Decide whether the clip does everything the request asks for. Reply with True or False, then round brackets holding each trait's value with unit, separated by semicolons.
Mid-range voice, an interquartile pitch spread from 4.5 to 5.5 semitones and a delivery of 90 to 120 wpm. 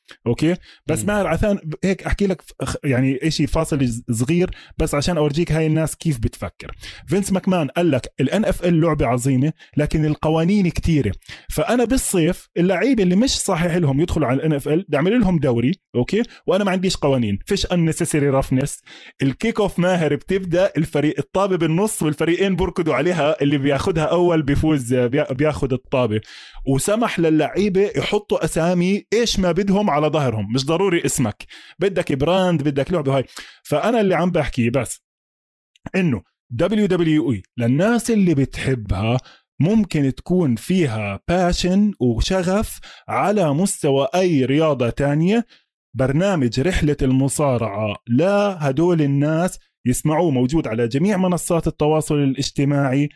False (155 Hz; 5.2 semitones; 135 wpm)